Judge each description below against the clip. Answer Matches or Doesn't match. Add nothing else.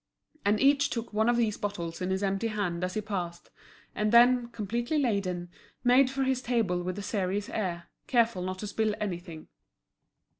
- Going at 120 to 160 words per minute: Doesn't match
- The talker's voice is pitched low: Doesn't match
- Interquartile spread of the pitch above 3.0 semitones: Matches